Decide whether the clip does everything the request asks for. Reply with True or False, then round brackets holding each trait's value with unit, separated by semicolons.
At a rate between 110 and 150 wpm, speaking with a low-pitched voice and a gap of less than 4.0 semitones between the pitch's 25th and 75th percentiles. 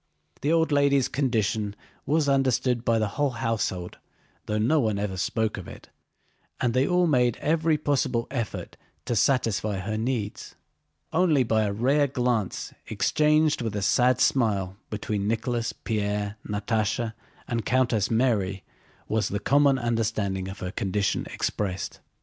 False (145 wpm; 115 Hz; 4.3 semitones)